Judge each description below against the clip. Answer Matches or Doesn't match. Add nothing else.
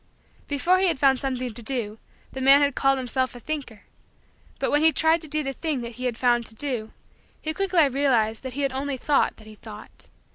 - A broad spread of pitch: Doesn't match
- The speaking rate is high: Matches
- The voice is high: Matches